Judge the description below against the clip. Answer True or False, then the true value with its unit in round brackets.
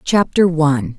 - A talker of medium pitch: True (160 Hz)